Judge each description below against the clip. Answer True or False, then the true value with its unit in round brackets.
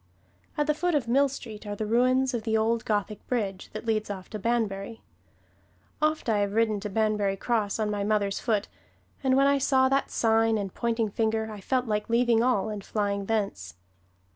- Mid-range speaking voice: False (220 Hz)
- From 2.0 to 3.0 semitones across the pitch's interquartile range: True (2.7 semitones)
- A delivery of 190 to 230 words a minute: True (195 wpm)